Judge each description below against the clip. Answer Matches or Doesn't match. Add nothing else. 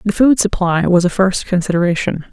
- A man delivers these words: Doesn't match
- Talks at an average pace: Matches